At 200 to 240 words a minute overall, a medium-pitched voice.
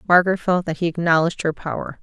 Yes: fast, 205 wpm; medium, 170 Hz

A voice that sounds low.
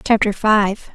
No: high, 210 Hz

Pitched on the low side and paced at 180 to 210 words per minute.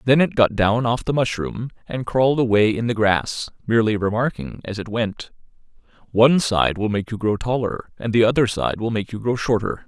Yes: low, 115 Hz; fast, 205 wpm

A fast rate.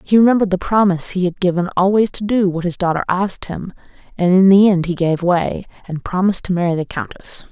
Yes: fast, 225 wpm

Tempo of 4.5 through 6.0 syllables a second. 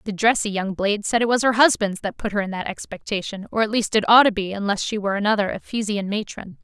No: 6.4 syllables/s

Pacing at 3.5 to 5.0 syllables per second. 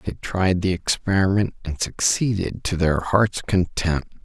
Yes: 4.1 syllables/s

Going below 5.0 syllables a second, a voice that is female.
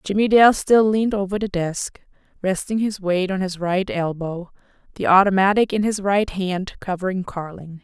Yes: 4.8 syllables/s; female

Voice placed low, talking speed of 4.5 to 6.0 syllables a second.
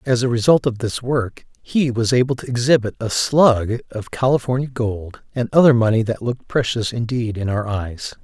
Yes: low, 120 Hz; 5.0 syllables/s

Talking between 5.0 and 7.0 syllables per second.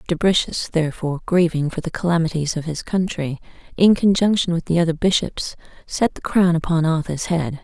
Yes: 5.5 syllables/s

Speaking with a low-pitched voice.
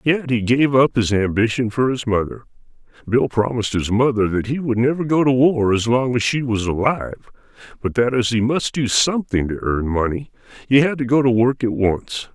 Yes: low, 120 Hz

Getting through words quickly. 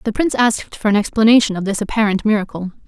Yes: fast, 210 wpm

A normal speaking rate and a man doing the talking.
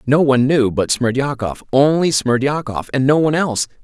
Yes: average, 170 wpm; male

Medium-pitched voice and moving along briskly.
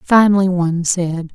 No: medium, 180 Hz; slow, 135 wpm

